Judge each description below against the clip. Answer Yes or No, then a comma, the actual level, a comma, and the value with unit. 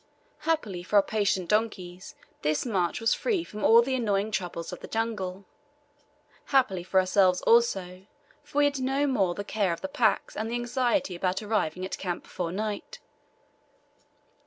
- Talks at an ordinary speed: Yes, average, 165 wpm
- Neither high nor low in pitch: No, high, 205 Hz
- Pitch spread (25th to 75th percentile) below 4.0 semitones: No, average, 4.3 semitones